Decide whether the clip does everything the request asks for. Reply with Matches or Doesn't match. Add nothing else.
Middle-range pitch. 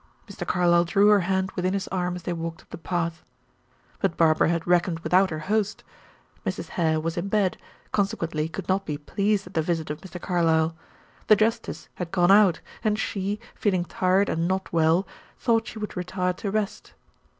Matches